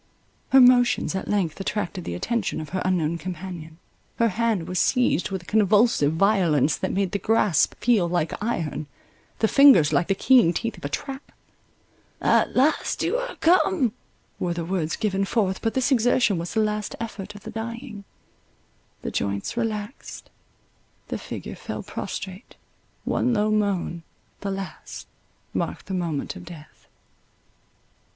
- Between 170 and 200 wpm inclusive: No, average, 145 wpm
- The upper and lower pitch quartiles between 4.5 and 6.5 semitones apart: Yes, average, 4.9 semitones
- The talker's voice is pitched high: Yes, high, 200 Hz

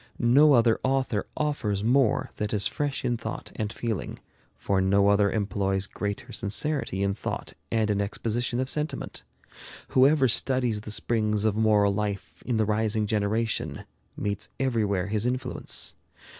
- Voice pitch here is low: Yes, low, 110 Hz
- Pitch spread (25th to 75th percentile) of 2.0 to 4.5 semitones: Yes, average, 3.4 semitones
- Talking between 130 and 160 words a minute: Yes, average, 145 wpm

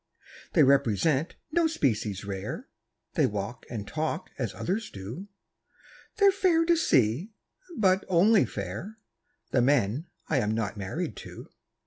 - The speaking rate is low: Yes, slow, 130 wpm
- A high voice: No, medium, 140 Hz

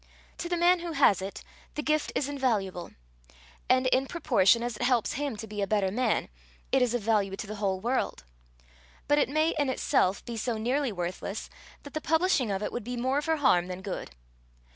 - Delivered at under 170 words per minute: No, fast, 205 wpm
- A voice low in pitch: No, high, 245 Hz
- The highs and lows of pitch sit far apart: Yes, wide, 6.0 semitones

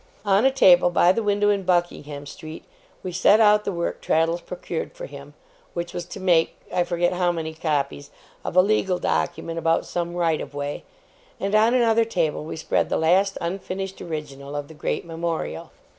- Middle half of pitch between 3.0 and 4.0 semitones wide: Yes, average, 3.6 semitones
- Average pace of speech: Yes, average, 190 wpm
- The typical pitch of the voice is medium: Yes, medium, 175 Hz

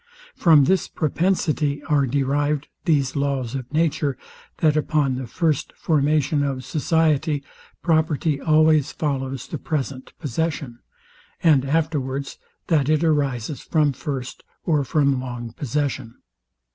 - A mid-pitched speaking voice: Yes, medium, 145 Hz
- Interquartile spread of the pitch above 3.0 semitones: No, narrow, 2.5 semitones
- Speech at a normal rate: No, slow, 120 wpm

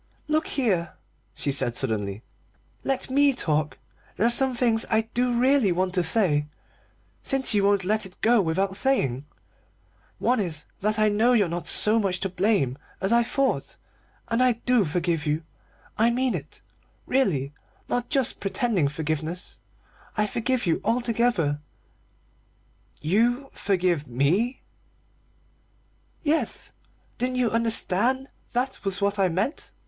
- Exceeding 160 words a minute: No, average, 145 wpm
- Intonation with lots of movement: Yes, wide, 6.3 semitones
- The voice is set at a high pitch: Yes, high, 210 Hz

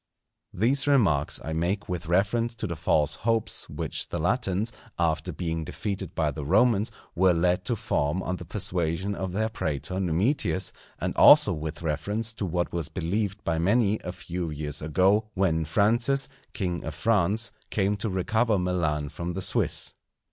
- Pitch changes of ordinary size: Yes, average, 4.5 semitones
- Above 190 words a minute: No, average, 165 wpm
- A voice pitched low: Yes, very low, 90 Hz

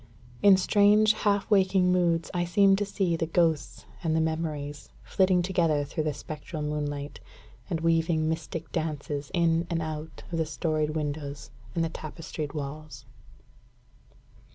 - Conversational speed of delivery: Yes, average, 145 wpm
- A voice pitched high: No, medium, 160 Hz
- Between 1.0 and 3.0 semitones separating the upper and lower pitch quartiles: Yes, average, 2.7 semitones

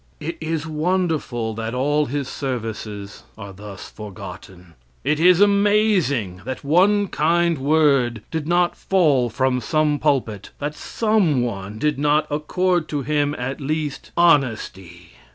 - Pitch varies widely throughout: Yes, wide, 5.7 semitones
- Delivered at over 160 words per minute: No, slow, 135 wpm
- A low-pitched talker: No, medium, 145 Hz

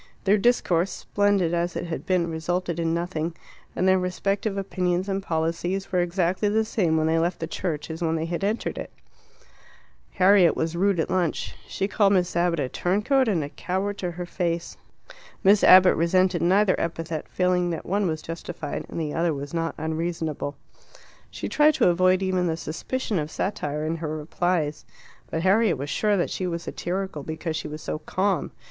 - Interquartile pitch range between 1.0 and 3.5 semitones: Yes, average, 2.7 semitones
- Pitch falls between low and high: Yes, medium, 175 Hz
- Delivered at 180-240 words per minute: Yes, average, 185 wpm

